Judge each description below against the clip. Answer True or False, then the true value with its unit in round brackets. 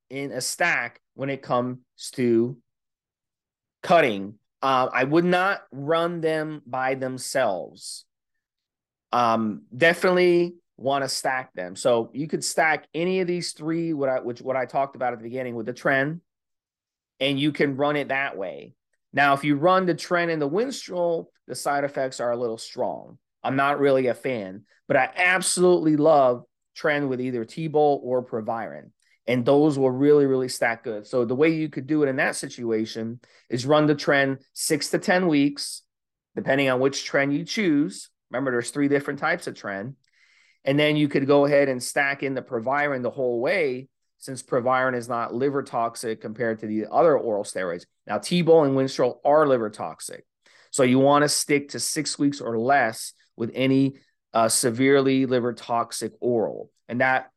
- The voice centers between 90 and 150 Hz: True (135 Hz)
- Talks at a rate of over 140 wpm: True (180 wpm)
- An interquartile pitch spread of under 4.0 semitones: True (3.5 semitones)